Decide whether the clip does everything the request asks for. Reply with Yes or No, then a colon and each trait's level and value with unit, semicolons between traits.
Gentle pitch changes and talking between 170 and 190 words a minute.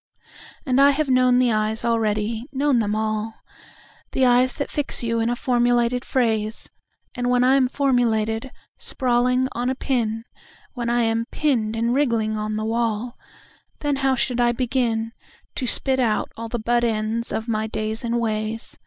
No: narrow, 2.3 semitones; average, 155 wpm